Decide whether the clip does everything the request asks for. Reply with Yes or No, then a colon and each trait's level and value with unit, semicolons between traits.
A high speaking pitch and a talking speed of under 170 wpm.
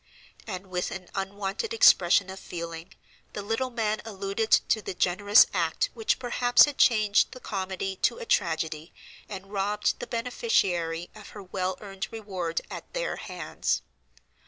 Yes: high, 195 Hz; average, 150 wpm